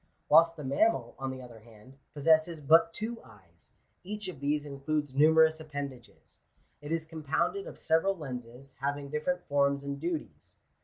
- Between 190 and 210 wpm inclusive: No, average, 155 wpm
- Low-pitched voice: No, medium, 145 Hz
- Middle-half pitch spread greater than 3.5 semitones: No, average, 3.1 semitones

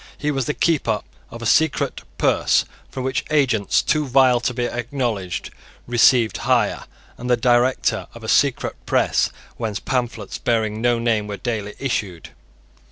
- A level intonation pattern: No, average, 3.0 semitones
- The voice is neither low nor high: No, low, 120 Hz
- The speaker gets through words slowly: No, average, 155 wpm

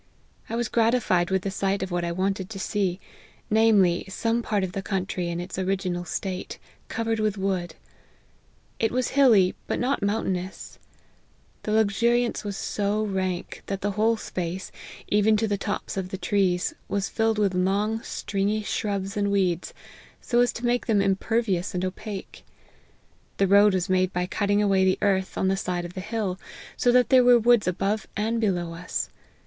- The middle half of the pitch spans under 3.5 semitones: Yes, average, 2.8 semitones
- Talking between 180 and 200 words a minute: Yes, average, 185 wpm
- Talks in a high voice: Yes, high, 200 Hz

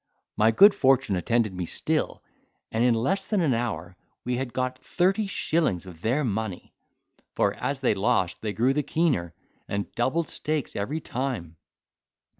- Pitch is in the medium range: No, low, 120 Hz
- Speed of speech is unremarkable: Yes, average, 160 wpm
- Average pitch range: No, wide, 6.2 semitones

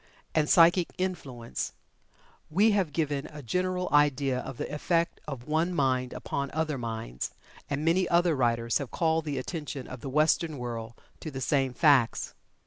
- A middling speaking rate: Yes, average, 160 wpm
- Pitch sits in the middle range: Yes, medium, 145 Hz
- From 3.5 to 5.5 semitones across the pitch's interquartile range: Yes, average, 4.4 semitones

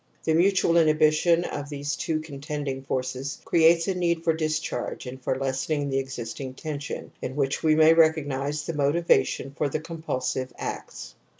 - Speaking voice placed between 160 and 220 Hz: No, medium, 150 Hz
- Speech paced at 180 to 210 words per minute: No, average, 170 wpm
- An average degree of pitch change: Yes, average, 3.0 semitones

